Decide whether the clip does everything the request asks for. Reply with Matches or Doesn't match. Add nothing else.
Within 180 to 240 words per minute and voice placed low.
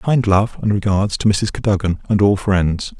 Matches